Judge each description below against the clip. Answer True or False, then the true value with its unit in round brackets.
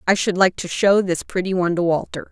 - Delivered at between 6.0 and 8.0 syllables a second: True (6.1 syllables/s)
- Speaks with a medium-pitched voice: True (180 Hz)